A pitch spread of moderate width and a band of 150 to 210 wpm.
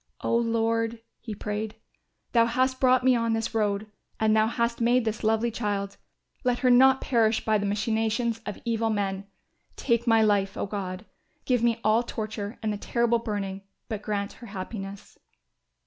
No: narrow, 2.1 semitones; average, 170 wpm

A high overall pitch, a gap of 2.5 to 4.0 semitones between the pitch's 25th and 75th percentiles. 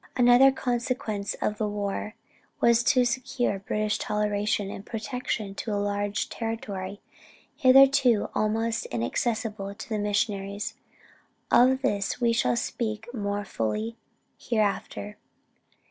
Yes: high, 215 Hz; average, 2.9 semitones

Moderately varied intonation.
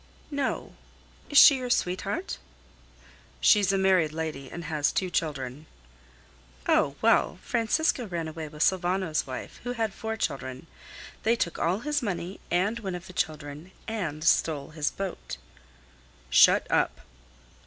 No: wide, 6.1 semitones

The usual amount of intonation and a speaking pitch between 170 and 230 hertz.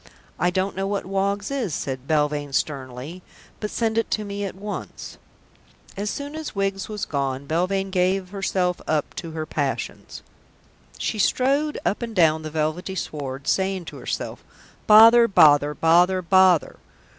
Yes: average, 4.6 semitones; medium, 185 Hz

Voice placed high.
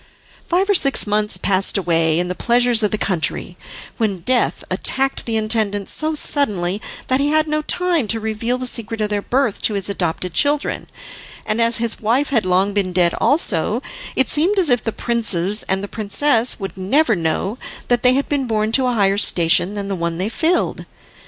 Yes: high, 220 Hz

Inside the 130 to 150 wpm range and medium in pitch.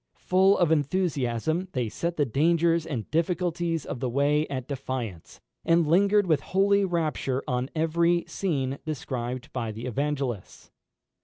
Yes: average, 140 wpm; medium, 150 Hz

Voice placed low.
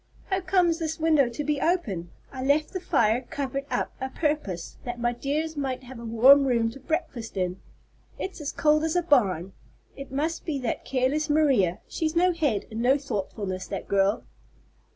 No: very high, 275 Hz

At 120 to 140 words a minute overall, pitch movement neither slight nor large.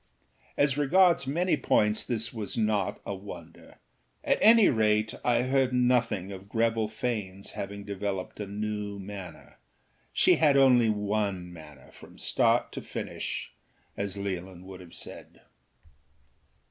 Yes: slow, 135 wpm; average, 4.1 semitones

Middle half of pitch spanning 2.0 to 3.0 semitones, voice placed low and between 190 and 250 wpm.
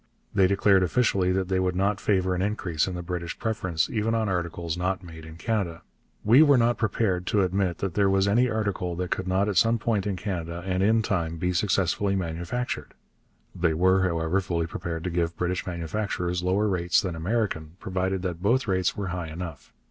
Yes: average, 2.7 semitones; very low, 95 Hz; average, 200 wpm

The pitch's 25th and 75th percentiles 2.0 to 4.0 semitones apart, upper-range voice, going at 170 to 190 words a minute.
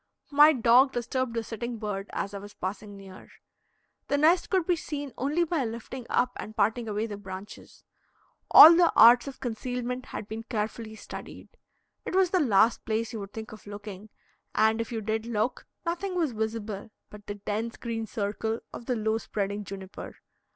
Yes: average, 3.4 semitones; high, 225 Hz; average, 180 wpm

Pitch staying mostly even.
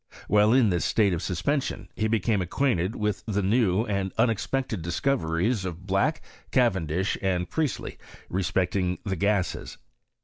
No: average, 3.7 semitones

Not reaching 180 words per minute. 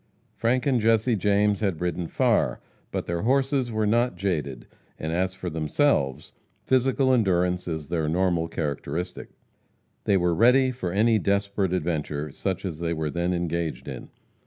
Yes: average, 155 wpm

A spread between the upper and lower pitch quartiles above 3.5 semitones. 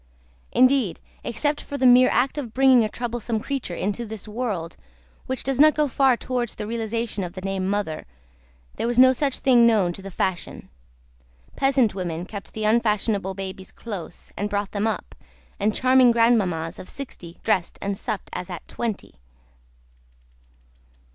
Yes: average, 4.4 semitones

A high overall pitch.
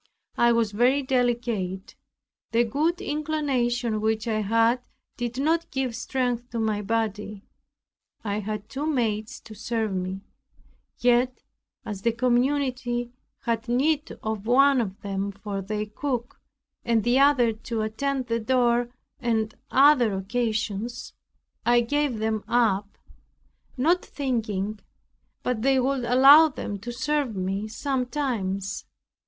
Yes: high, 235 Hz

